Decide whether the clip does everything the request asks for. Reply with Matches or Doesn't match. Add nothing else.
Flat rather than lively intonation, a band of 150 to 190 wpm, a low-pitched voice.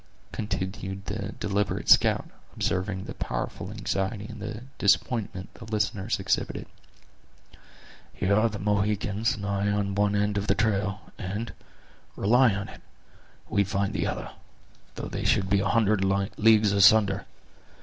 Doesn't match